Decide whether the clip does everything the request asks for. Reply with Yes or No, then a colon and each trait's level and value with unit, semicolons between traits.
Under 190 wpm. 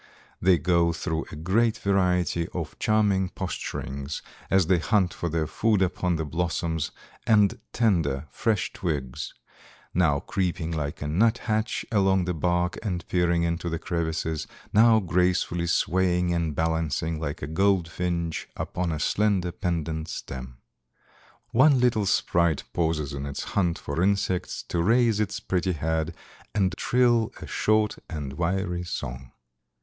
Yes: average, 140 wpm